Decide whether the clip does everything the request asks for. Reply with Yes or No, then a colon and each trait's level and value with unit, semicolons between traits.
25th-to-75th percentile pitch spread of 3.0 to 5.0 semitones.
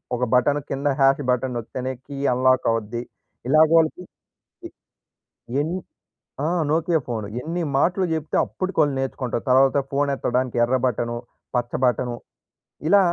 Yes: average, 3.8 semitones